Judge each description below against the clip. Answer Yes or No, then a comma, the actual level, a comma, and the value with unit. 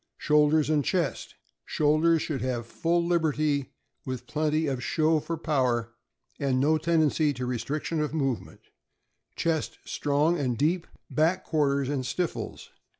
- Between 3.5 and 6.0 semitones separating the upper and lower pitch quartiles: No, average, 2.8 semitones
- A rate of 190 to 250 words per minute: No, average, 145 wpm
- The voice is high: No, medium, 150 Hz